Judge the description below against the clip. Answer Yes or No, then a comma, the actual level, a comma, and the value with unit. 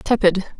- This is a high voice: Yes, high, 205 Hz